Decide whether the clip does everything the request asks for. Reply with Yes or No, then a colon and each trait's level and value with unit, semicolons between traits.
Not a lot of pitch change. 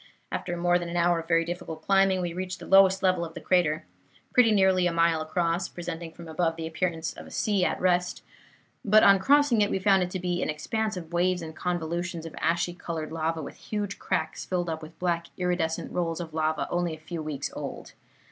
Yes: narrow, 2.0 semitones